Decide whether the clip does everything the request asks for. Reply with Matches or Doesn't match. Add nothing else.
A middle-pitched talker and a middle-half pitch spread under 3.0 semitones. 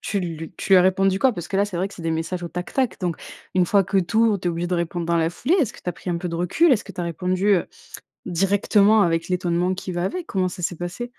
Matches